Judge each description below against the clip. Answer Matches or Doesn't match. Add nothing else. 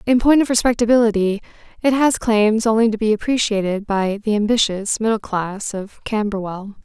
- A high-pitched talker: Matches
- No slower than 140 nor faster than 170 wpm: Matches